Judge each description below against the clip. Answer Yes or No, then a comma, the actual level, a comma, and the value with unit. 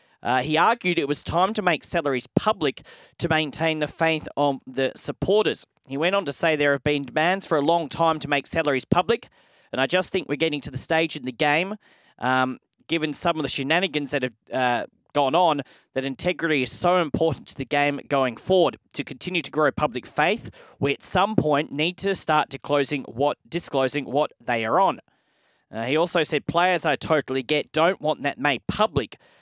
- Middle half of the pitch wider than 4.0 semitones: No, average, 3.4 semitones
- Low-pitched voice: No, medium, 150 Hz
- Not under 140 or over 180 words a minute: No, fast, 205 wpm